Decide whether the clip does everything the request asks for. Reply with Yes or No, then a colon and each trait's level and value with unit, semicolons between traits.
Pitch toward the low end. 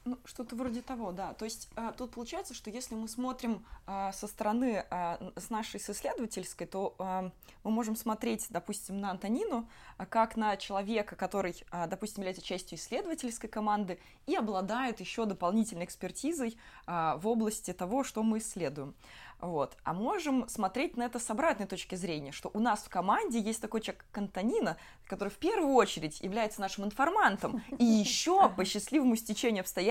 No: high, 215 Hz